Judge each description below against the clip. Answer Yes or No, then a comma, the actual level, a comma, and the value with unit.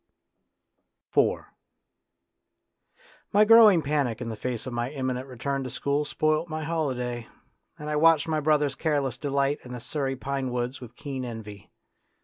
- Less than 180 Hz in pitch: Yes, medium, 140 Hz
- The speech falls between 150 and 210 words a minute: Yes, average, 155 wpm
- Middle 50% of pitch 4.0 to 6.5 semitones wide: No, average, 3.4 semitones